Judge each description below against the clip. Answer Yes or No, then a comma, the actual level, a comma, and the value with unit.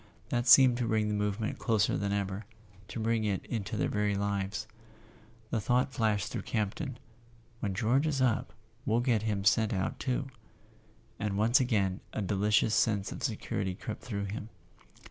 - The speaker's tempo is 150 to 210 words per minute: Yes, average, 170 wpm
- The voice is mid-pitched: No, low, 110 Hz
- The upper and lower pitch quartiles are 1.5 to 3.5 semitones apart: Yes, average, 2.8 semitones